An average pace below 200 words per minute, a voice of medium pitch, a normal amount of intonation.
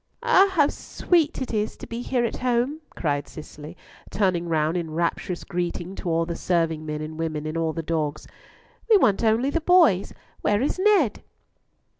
No: average, 170 wpm; medium, 180 Hz; wide, 7.5 semitones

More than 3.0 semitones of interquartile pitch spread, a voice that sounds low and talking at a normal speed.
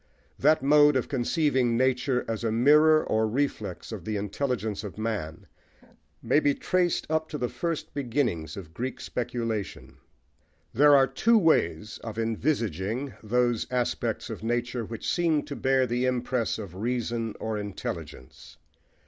Yes: average, 4.4 semitones; low, 120 Hz; average, 145 wpm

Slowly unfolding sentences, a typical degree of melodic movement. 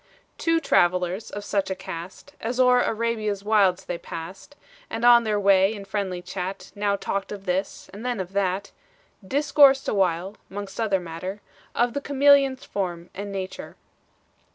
No: average, 155 wpm; average, 3.7 semitones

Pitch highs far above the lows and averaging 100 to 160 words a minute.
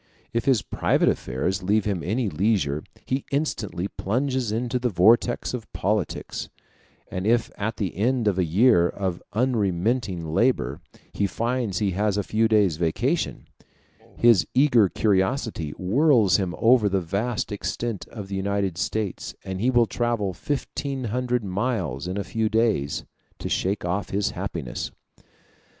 No: average, 4.2 semitones; average, 150 wpm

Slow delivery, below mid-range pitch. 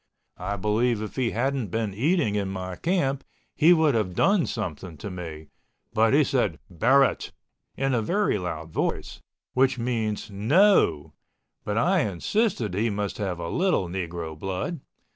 No: average, 160 wpm; low, 110 Hz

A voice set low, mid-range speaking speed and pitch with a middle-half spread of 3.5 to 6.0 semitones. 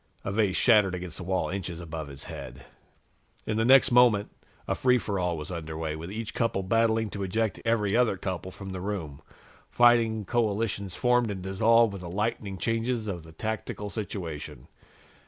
Yes: low, 100 Hz; average, 180 wpm; average, 4.1 semitones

